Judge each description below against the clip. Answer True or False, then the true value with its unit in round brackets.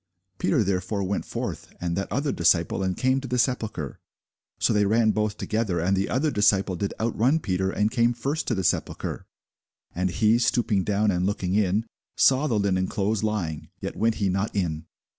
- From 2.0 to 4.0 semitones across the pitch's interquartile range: True (3.5 semitones)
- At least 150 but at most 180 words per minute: False (190 wpm)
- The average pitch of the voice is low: True (105 Hz)